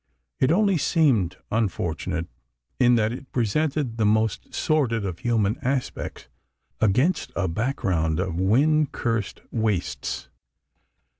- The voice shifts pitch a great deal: Yes, wide, 6.0 semitones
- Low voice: Yes, low, 115 Hz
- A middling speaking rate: No, slow, 115 wpm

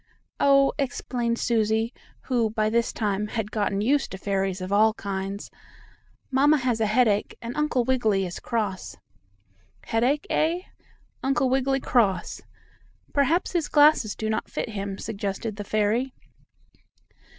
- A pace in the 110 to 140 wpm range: Yes, slow, 135 wpm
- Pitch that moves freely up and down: No, average, 4.2 semitones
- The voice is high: Yes, high, 225 Hz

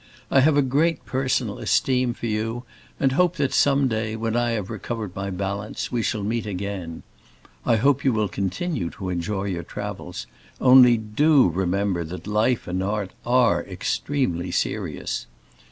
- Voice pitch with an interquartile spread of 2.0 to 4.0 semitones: No, average, 4.8 semitones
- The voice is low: Yes, low, 110 Hz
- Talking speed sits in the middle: Yes, average, 160 wpm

